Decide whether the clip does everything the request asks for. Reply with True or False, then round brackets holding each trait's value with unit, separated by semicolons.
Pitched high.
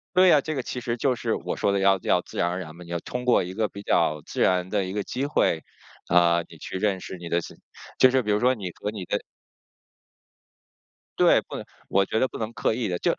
False (100 Hz)